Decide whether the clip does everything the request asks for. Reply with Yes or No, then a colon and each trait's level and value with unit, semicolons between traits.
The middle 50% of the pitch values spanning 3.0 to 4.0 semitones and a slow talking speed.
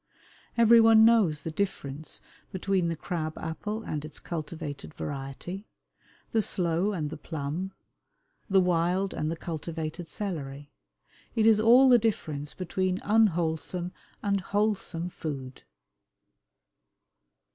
No: average, 4.5 semitones; slow, 115 wpm